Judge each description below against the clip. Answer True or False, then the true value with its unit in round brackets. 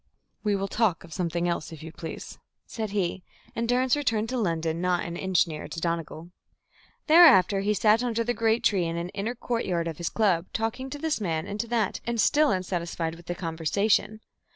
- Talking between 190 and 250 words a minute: True (200 wpm)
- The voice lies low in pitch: False (195 Hz)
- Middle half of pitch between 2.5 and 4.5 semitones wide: False (5.1 semitones)